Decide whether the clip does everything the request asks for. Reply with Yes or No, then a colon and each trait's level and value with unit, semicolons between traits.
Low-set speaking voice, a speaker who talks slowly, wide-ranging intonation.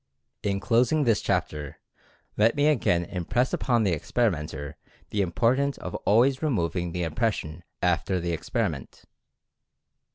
Yes: low, 100 Hz; slow, 125 wpm; wide, 6.0 semitones